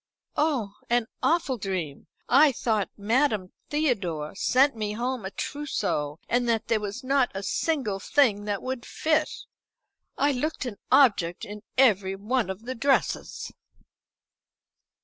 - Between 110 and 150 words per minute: Yes, slow, 135 wpm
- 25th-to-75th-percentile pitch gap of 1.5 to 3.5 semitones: No, average, 5.2 semitones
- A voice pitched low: No, high, 230 Hz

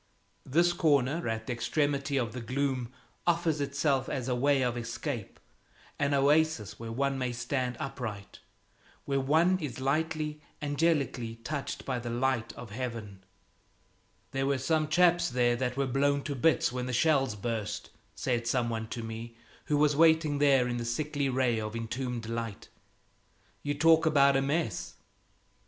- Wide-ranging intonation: No, average, 3.5 semitones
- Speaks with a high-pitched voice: No, low, 135 Hz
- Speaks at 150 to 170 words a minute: Yes, average, 160 wpm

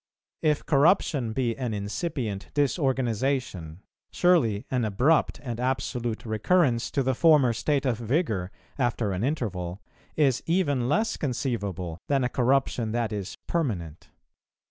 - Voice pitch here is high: No, low, 125 Hz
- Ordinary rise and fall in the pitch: Yes, average, 4.7 semitones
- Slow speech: Yes, slow, 125 wpm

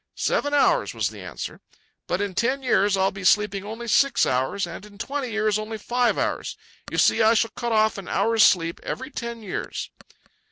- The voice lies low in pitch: No, high, 215 Hz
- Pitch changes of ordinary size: Yes, average, 3.1 semitones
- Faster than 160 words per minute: Yes, average, 195 wpm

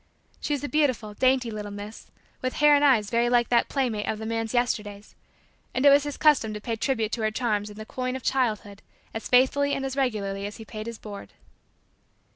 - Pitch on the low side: No, high, 230 Hz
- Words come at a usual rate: No, fast, 220 wpm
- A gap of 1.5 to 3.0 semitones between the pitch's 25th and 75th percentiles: No, average, 3.6 semitones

